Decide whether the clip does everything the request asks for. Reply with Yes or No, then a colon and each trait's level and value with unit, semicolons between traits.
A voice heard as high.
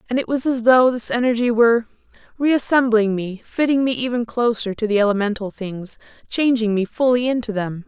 Yes: high, 230 Hz